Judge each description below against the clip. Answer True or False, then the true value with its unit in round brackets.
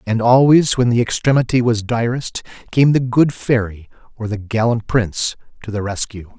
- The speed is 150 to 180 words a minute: True (170 wpm)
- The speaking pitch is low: True (115 Hz)